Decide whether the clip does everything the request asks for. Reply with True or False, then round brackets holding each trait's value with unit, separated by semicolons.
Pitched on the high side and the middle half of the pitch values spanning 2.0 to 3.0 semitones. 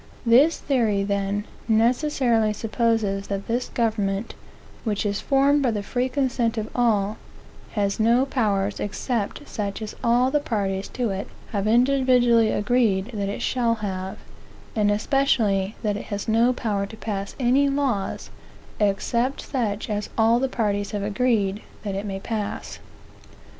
False (220 Hz; 3.4 semitones)